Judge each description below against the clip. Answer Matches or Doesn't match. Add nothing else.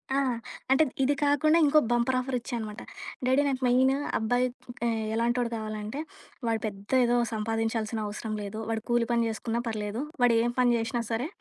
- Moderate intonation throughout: Doesn't match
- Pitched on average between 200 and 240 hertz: Matches